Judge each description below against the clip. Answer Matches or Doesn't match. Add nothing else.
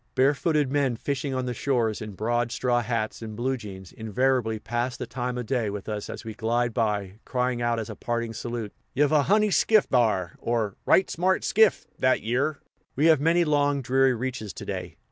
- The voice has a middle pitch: Doesn't match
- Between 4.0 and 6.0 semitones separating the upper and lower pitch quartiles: Doesn't match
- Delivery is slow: Doesn't match